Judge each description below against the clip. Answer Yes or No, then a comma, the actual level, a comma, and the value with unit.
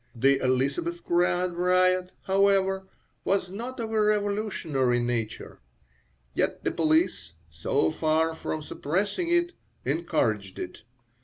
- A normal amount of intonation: No, wide, 6.7 semitones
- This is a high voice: No, medium, 180 Hz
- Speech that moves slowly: Yes, slow, 105 wpm